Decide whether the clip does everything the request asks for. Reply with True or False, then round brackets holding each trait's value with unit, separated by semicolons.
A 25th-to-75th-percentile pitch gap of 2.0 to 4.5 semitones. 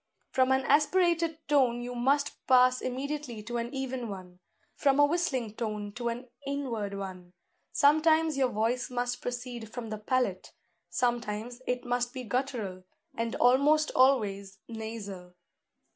True (3.7 semitones)